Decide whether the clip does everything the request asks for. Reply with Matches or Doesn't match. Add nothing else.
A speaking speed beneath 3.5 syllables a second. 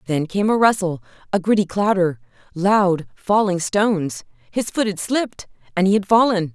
Doesn't match